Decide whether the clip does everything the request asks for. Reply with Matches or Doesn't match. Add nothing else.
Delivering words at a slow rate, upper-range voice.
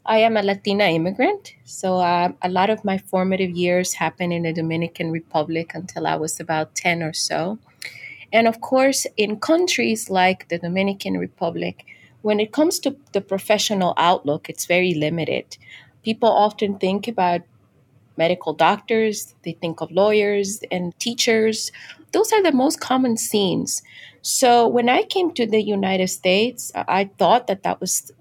Doesn't match